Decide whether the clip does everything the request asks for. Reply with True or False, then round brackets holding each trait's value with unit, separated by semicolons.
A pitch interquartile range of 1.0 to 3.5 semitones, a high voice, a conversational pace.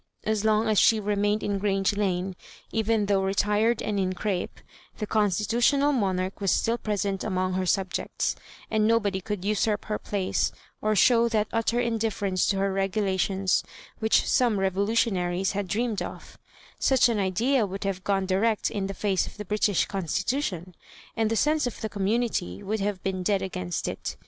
True (2.4 semitones; 205 Hz; 175 wpm)